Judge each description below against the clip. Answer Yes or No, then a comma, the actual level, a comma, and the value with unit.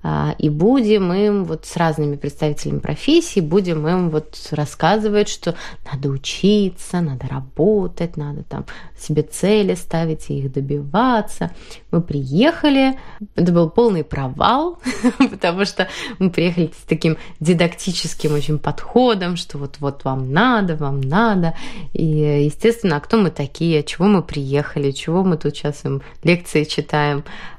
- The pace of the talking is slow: No, average, 135 wpm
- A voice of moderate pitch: Yes, medium, 165 Hz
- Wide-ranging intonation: Yes, wide, 5.8 semitones